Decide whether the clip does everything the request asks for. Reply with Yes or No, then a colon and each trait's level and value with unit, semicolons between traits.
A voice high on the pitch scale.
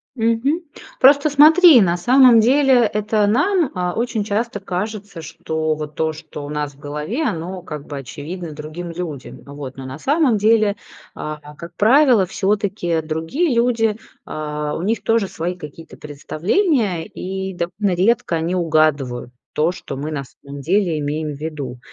No: medium, 180 Hz